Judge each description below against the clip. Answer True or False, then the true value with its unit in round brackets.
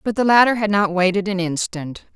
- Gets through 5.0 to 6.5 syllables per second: True (5.5 syllables/s)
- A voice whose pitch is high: True (195 Hz)